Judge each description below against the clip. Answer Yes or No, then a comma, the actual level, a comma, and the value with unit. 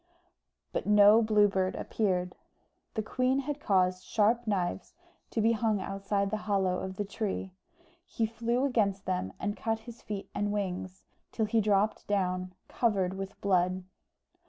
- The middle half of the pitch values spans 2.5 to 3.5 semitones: Yes, average, 2.8 semitones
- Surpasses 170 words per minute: No, average, 155 wpm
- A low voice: No, high, 205 Hz